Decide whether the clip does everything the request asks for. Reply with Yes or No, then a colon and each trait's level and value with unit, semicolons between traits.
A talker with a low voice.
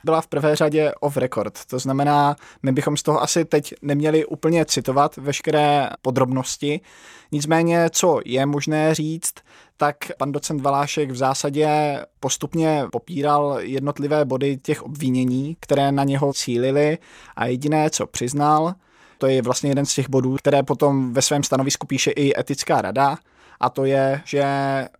No: medium, 145 Hz